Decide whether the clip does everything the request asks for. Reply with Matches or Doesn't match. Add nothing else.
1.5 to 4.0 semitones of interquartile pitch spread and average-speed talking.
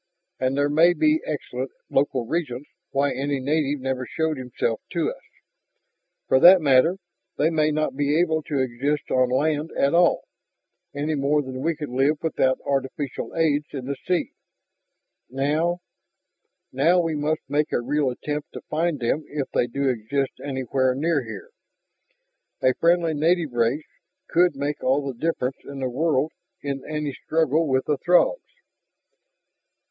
Matches